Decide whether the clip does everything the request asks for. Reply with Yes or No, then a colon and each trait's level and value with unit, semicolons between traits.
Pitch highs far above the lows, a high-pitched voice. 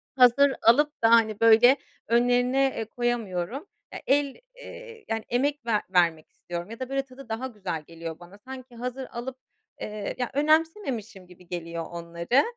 Yes: wide, 5.8 semitones; high, 240 Hz